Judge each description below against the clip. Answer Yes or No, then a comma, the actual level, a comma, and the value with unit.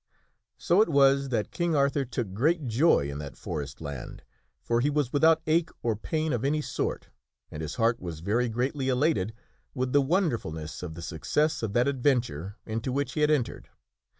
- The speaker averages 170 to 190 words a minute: Yes, average, 185 wpm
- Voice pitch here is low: Yes, low, 125 Hz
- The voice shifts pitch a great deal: Yes, wide, 6.5 semitones